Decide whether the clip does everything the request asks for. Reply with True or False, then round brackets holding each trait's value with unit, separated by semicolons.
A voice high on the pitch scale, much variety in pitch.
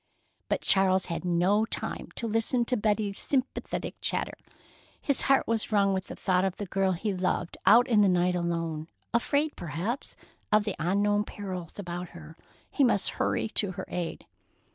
False (195 Hz; 3.6 semitones)